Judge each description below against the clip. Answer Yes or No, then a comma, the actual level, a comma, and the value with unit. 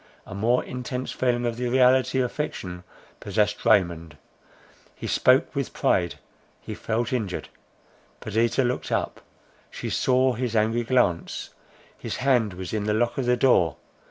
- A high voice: No, low, 120 Hz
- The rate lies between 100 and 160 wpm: Yes, average, 150 wpm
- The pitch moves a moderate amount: Yes, average, 3.7 semitones